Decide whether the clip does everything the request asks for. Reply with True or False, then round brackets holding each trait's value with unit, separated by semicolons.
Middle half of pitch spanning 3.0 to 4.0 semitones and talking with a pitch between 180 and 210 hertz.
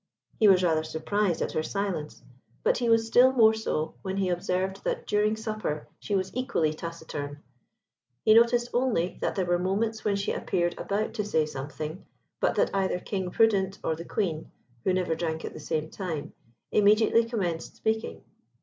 False (4.9 semitones; 190 Hz)